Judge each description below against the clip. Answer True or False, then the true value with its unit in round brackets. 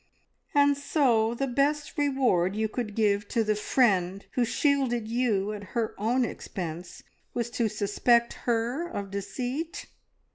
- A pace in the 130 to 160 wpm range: True (140 wpm)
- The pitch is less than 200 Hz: False (235 Hz)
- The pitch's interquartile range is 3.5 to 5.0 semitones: True (4.1 semitones)